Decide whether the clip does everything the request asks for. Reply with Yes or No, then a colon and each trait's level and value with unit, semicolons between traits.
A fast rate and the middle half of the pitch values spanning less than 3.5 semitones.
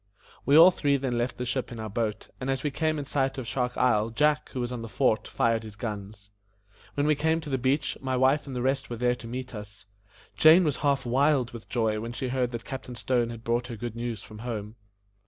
Yes: fast, 245 wpm; average, 2.9 semitones